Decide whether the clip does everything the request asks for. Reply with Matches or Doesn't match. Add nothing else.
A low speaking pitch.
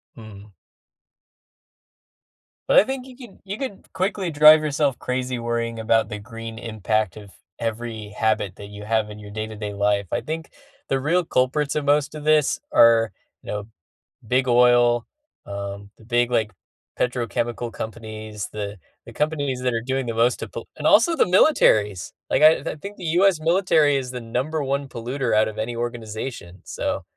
Matches